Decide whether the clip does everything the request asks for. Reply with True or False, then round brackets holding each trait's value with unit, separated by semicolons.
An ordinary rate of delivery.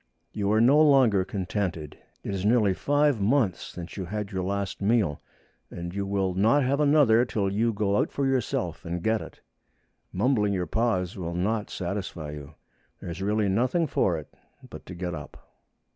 True (180 wpm)